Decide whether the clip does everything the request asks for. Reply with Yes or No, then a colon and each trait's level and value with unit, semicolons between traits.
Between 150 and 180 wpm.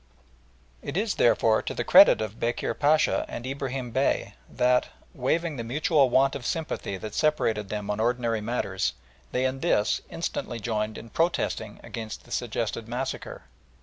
Yes: average, 155 wpm